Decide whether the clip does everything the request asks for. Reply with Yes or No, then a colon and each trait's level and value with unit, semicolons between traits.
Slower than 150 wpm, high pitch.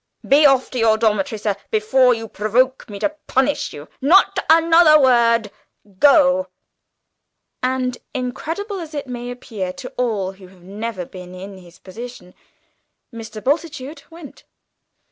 Yes: average, 140 wpm; high, 245 Hz